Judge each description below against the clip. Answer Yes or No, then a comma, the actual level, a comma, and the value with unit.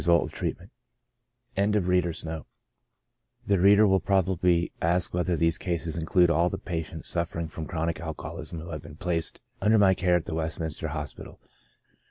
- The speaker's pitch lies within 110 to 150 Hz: No, very low, 85 Hz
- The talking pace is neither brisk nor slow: Yes, average, 165 wpm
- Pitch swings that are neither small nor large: No, narrow, 1.9 semitones